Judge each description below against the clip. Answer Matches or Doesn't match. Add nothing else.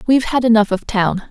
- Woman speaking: Matches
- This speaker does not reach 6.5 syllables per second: Matches